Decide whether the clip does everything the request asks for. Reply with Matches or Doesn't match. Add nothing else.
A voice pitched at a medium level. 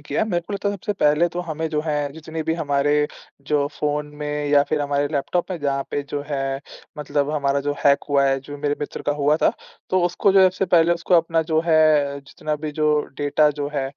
Matches